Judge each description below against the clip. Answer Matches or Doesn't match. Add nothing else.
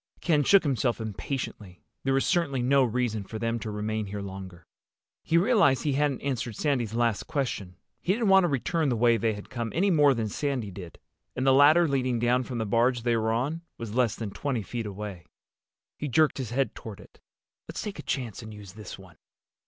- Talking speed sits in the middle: Doesn't match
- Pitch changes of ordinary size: Matches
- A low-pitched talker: Matches